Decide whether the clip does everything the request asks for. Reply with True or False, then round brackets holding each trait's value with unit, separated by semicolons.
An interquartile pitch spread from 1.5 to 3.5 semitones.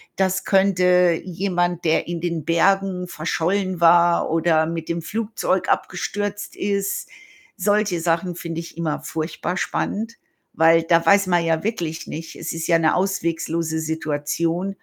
True (2.6 semitones)